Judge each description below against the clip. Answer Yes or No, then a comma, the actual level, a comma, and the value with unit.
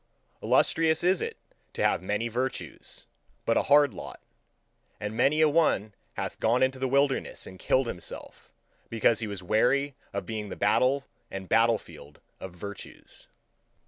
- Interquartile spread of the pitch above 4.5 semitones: Yes, average, 5.0 semitones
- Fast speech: No, average, 150 wpm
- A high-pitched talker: No, low, 115 Hz